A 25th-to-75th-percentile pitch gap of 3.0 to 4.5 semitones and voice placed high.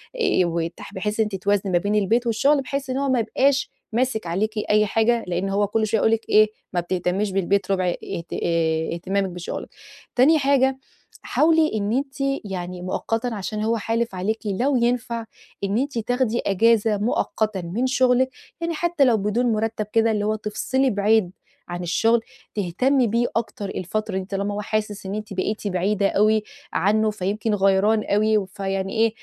Yes: average, 3.3 semitones; high, 215 Hz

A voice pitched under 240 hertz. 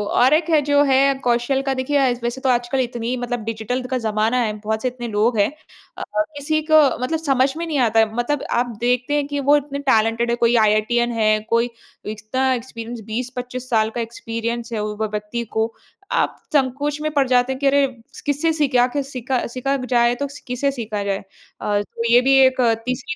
No: high, 245 Hz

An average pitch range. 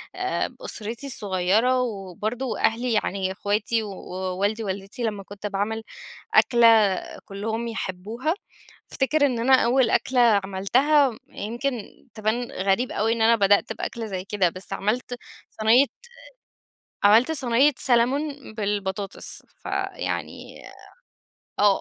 Yes: average, 3.7 semitones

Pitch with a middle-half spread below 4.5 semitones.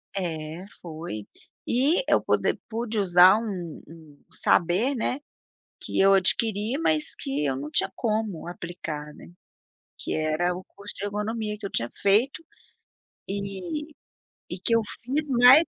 No: wide, 5.6 semitones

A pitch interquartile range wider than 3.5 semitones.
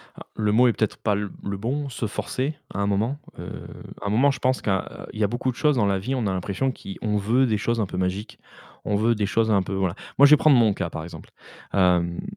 Yes: average, 4.2 semitones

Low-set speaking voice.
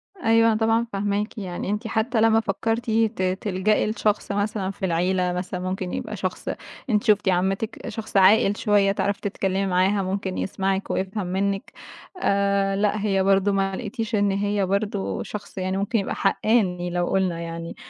No: high, 200 Hz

